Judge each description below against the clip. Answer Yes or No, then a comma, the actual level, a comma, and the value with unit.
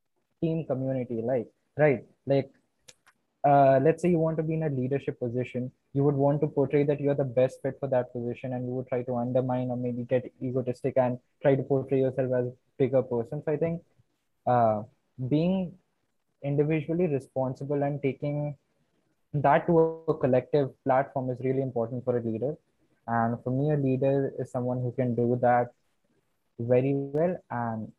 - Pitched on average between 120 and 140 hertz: Yes, low, 135 Hz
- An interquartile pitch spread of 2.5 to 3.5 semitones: Yes, average, 2.8 semitones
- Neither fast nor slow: Yes, average, 175 wpm